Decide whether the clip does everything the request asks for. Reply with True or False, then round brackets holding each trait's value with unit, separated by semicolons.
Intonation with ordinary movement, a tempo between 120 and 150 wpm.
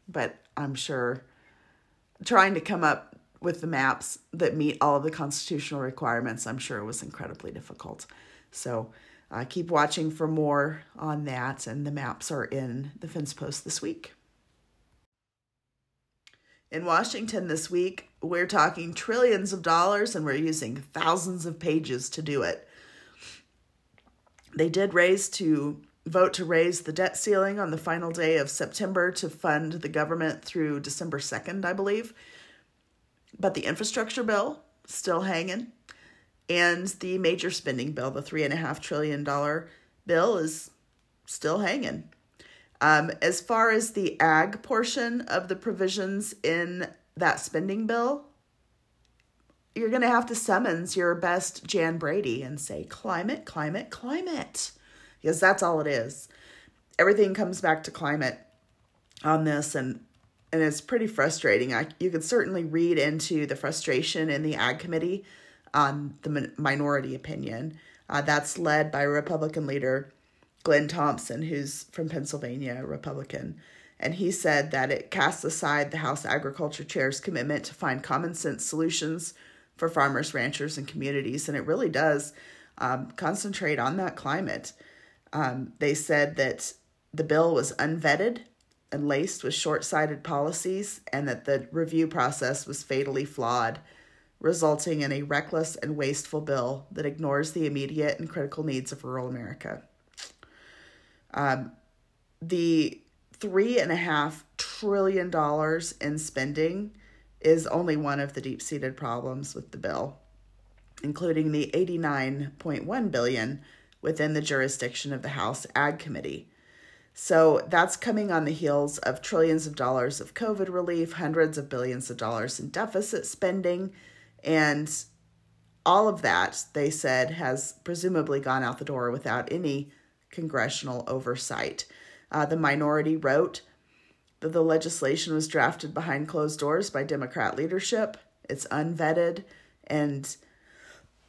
True (3.5 semitones; 140 wpm)